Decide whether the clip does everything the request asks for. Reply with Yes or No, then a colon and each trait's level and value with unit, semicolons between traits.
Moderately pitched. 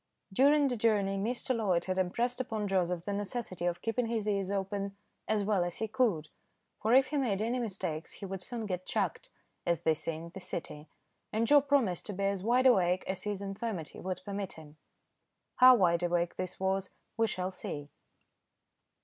No: high, 195 Hz